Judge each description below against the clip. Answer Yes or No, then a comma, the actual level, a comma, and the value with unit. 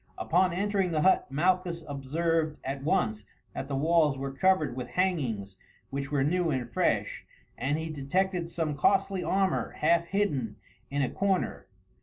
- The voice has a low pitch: No, medium, 160 Hz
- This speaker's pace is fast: No, average, 155 wpm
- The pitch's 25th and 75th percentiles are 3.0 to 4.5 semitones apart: No, average, 4.9 semitones